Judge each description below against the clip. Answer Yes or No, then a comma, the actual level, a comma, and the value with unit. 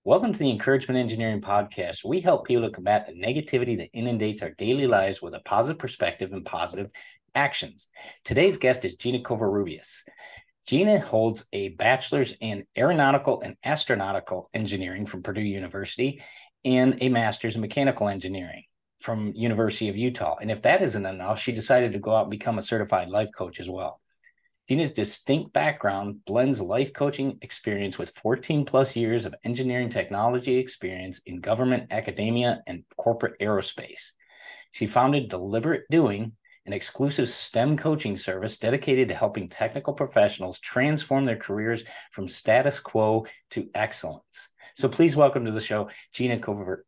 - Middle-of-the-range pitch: No, low, 115 Hz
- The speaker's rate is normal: Yes, average, 155 wpm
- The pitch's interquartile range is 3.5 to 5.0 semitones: Yes, average, 4.0 semitones